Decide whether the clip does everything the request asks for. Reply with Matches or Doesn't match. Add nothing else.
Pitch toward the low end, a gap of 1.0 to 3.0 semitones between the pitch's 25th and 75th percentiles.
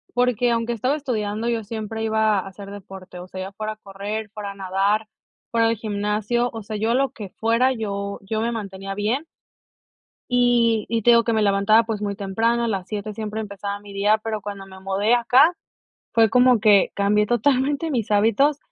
Doesn't match